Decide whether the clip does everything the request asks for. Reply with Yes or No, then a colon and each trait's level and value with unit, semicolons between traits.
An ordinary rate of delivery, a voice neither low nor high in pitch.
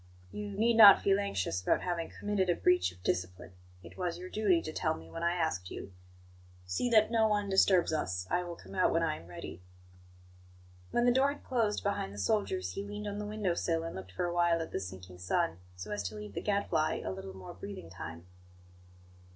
No: fast, 220 wpm; medium, 170 Hz